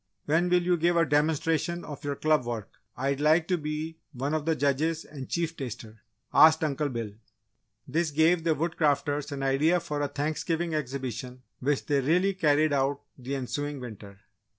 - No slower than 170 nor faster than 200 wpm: Yes, average, 175 wpm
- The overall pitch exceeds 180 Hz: No, medium, 150 Hz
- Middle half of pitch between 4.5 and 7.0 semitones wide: No, average, 2.9 semitones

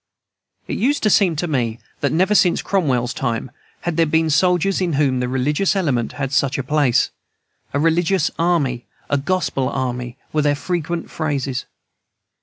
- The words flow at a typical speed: Yes, average, 165 wpm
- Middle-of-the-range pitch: Yes, medium, 150 Hz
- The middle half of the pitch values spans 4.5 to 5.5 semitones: Yes, average, 4.9 semitones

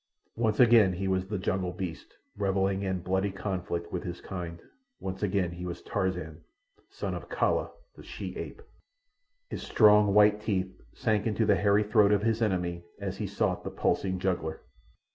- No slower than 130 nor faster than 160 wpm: No, average, 170 wpm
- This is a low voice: Yes, very low, 95 Hz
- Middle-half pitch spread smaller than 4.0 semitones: Yes, narrow, 2.6 semitones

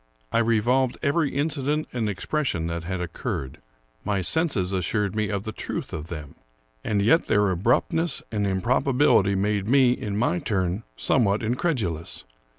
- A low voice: Yes, low, 105 Hz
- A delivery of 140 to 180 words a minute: Yes, average, 155 wpm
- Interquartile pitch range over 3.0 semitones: Yes, wide, 5.4 semitones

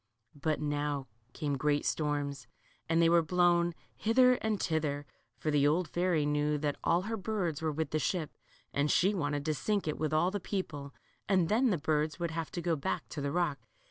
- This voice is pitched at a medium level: Yes, medium, 155 Hz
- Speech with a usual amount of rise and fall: Yes, average, 3.2 semitones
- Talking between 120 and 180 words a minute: No, fast, 205 wpm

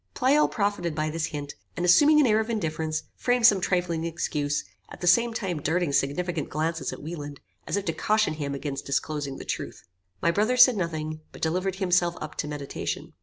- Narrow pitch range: No, average, 4.8 semitones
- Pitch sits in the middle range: Yes, medium, 170 Hz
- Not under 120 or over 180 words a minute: No, average, 195 wpm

